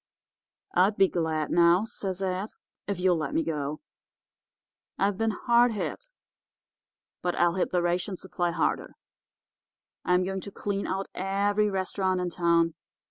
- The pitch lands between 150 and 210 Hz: Yes, medium, 185 Hz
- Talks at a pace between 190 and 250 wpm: No, average, 140 wpm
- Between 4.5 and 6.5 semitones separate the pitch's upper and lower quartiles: No, narrow, 2.4 semitones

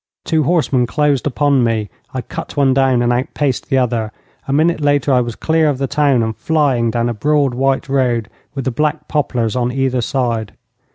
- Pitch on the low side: Yes, low, 130 Hz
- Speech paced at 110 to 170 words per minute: No, average, 195 wpm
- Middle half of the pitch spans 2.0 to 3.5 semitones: Yes, average, 3.2 semitones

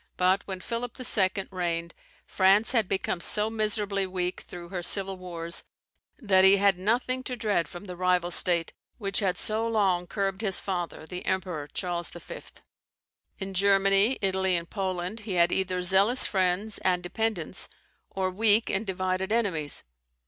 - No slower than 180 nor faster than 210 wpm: No, average, 155 wpm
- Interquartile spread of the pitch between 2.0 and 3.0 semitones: Yes, narrow, 2.5 semitones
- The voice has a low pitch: No, high, 190 Hz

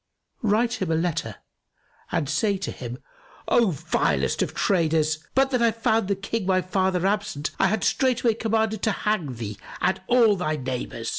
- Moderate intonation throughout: No, wide, 6.1 semitones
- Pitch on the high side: Yes, high, 195 Hz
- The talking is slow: No, average, 170 wpm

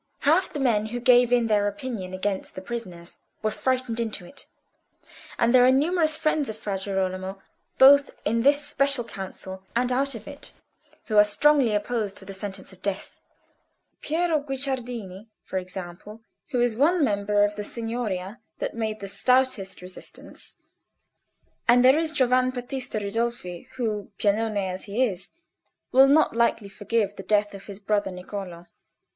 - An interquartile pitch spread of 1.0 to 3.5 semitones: No, average, 4.4 semitones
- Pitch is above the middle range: Yes, high, 225 Hz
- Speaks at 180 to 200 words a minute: No, average, 160 wpm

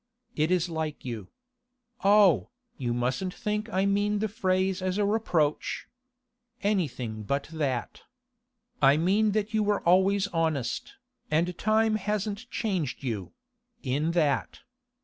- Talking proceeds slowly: Yes, slow, 125 wpm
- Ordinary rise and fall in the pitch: No, wide, 5.9 semitones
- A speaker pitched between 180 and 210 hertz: Yes, medium, 185 Hz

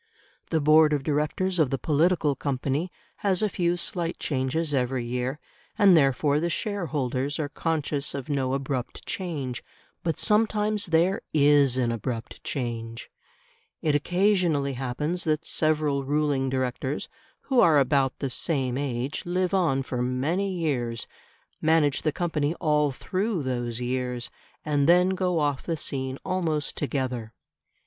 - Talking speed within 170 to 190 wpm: No, average, 140 wpm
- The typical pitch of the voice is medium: Yes, medium, 145 Hz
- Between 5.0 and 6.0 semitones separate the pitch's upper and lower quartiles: No, average, 4.3 semitones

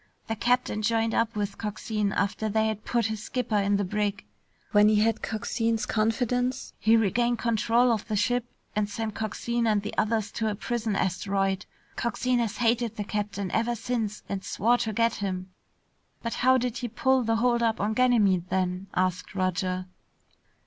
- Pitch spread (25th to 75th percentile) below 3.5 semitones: Yes, narrow, 2.5 semitones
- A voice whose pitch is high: Yes, high, 220 Hz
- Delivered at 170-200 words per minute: Yes, average, 175 wpm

